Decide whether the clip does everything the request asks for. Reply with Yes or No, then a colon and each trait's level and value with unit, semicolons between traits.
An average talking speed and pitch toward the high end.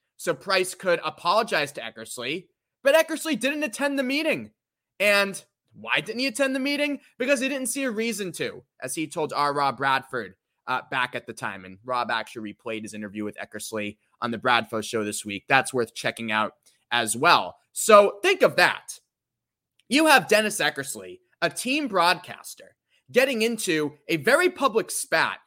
Yes: average, 175 wpm; high, 200 Hz